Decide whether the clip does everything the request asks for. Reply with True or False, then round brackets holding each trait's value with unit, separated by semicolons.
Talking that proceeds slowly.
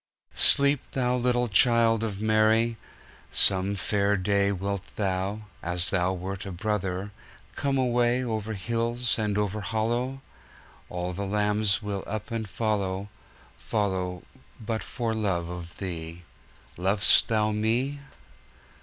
True (110 wpm)